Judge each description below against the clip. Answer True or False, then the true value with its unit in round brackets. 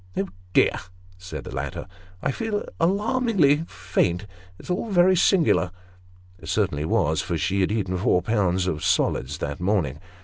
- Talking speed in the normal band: True (165 wpm)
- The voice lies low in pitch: True (95 Hz)